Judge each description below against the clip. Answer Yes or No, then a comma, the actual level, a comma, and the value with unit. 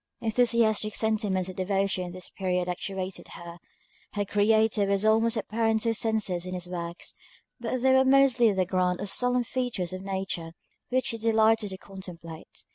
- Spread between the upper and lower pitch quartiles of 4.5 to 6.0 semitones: No, average, 3.5 semitones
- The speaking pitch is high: Yes, high, 205 Hz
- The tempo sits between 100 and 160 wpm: No, average, 170 wpm